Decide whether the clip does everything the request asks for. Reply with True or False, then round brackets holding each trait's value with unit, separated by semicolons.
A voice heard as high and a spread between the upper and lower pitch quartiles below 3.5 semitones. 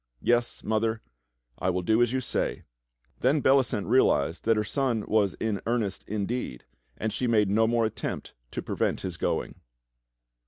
False (110 Hz; 3.0 semitones)